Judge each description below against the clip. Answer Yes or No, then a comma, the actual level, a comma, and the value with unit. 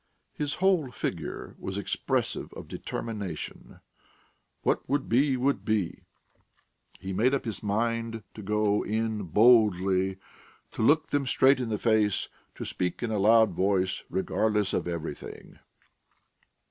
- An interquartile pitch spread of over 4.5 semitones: No, average, 3.9 semitones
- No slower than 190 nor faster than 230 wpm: No, slow, 135 wpm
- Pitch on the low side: Yes, low, 110 Hz